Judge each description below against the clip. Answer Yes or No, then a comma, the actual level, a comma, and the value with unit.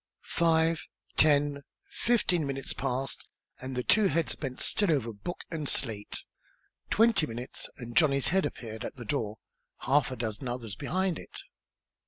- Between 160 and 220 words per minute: No, average, 150 wpm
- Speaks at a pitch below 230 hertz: Yes, medium, 140 Hz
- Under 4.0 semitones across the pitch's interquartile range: No, average, 5.2 semitones